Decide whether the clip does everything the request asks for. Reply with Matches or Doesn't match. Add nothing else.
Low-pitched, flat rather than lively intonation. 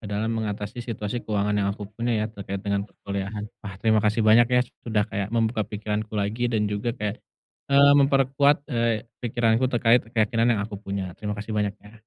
Matches